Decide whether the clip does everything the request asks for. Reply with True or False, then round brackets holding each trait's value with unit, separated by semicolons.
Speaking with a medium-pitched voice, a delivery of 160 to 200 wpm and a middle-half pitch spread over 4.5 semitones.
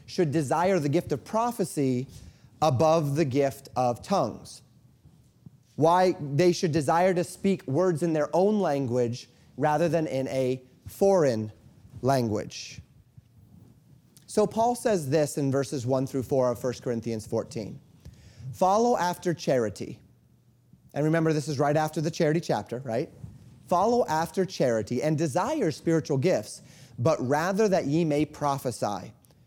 False (150 Hz; 135 wpm; 5.2 semitones)